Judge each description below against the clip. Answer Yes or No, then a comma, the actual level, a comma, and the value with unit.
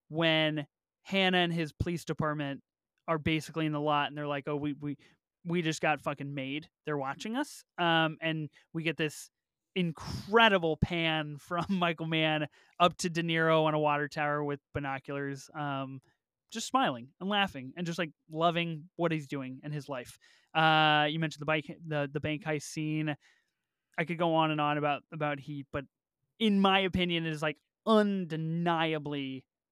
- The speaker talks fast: No, average, 175 wpm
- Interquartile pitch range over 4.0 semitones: No, narrow, 2.5 semitones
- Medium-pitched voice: Yes, medium, 155 Hz